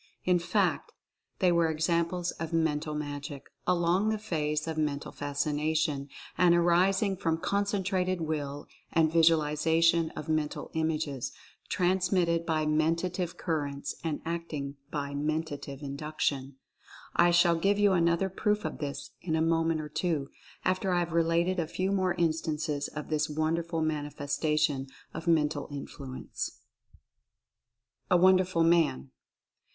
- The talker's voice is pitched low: No, medium, 160 Hz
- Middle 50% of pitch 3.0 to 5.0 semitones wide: No, narrow, 2.5 semitones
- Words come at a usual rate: No, slow, 130 wpm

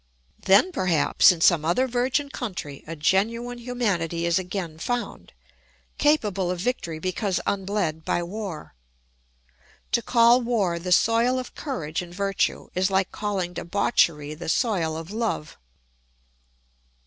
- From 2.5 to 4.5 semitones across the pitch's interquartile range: No, wide, 5.6 semitones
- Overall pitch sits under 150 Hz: No, high, 190 Hz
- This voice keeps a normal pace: No, slow, 130 wpm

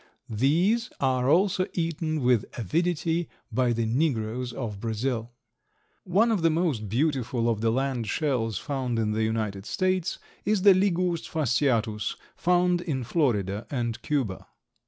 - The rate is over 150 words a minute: No, slow, 135 wpm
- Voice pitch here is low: Yes, low, 130 Hz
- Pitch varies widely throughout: Yes, wide, 6.8 semitones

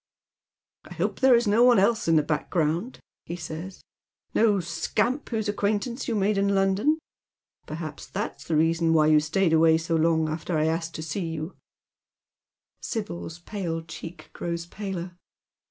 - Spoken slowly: No, average, 170 wpm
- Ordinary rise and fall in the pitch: Yes, average, 4.2 semitones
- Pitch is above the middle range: No, medium, 170 Hz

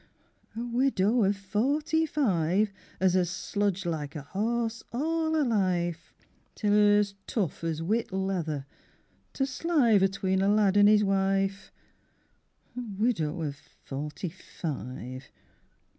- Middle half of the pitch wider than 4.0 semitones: Yes, average, 4.8 semitones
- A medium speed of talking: No, slow, 125 wpm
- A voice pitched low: No, high, 195 Hz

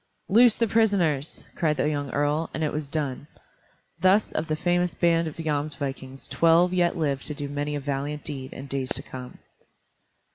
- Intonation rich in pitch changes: No, average, 3.1 semitones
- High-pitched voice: No, medium, 150 Hz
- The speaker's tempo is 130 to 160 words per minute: No, average, 180 wpm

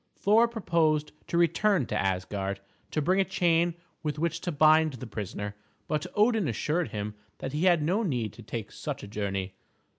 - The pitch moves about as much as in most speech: No, wide, 8.6 semitones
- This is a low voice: No, medium, 155 Hz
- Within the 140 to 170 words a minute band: No, average, 180 wpm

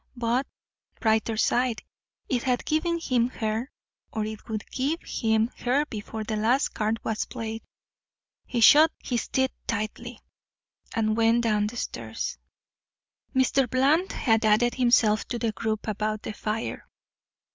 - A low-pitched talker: No, high, 230 Hz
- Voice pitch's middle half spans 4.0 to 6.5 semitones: No, average, 2.7 semitones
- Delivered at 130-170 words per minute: Yes, average, 140 wpm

